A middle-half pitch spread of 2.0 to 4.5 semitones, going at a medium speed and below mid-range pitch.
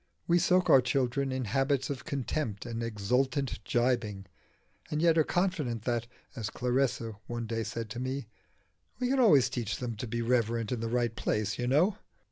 Yes: average, 3.1 semitones; average, 180 wpm; low, 125 Hz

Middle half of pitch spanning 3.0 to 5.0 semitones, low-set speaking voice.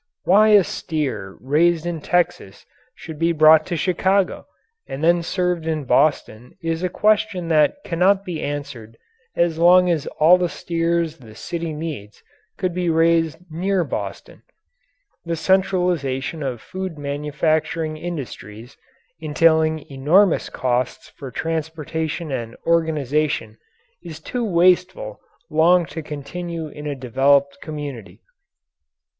No: average, 3.3 semitones; medium, 160 Hz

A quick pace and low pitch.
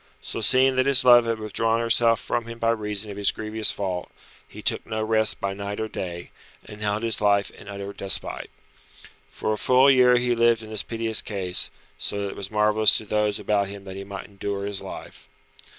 Yes: fast, 215 wpm; low, 105 Hz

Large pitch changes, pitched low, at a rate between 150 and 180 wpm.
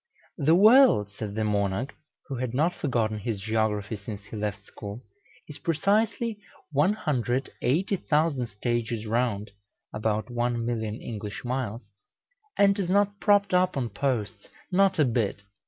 No: wide, 7.6 semitones; low, 120 Hz; slow, 135 wpm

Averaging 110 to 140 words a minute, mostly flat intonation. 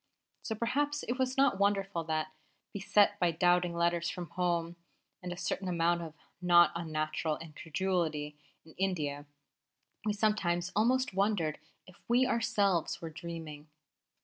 No: slow, 135 wpm; average, 3.7 semitones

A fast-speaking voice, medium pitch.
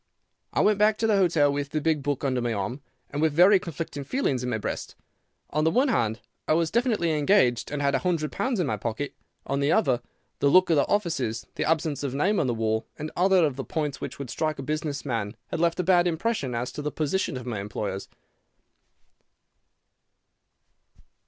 Yes: fast, 210 wpm; medium, 150 Hz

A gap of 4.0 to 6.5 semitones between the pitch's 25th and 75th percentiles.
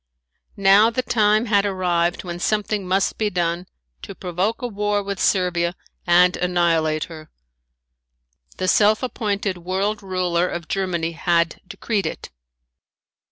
No: average, 3.1 semitones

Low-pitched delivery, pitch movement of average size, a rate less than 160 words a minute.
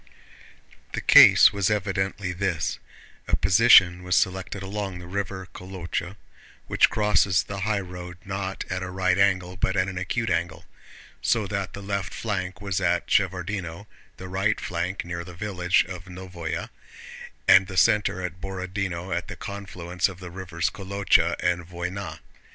No: very low, 95 Hz; narrow, 1.9 semitones; average, 145 wpm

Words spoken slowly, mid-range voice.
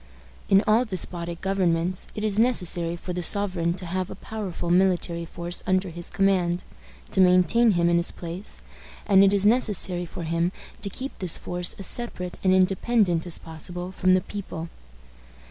No: average, 170 wpm; medium, 180 Hz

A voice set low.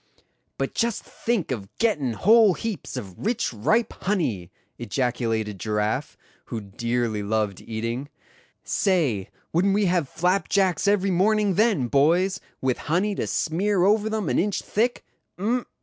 No: medium, 175 Hz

